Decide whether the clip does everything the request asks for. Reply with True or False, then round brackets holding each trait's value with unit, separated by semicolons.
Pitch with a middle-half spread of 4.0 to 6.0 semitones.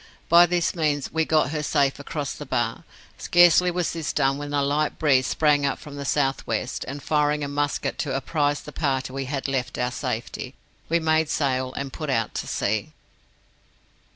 False (2.4 semitones)